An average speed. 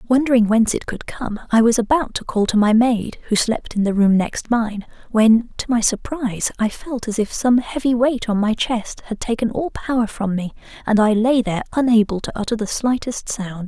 No: fast, 220 wpm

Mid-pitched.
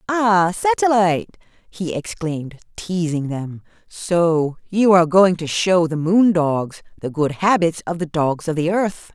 Yes: medium, 170 Hz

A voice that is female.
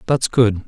No: male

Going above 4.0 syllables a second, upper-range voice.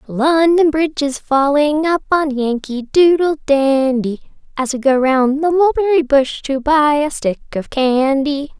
No: 3.9 syllables/s; very high, 285 Hz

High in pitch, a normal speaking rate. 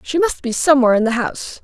No: very high, 260 Hz; fast, 255 wpm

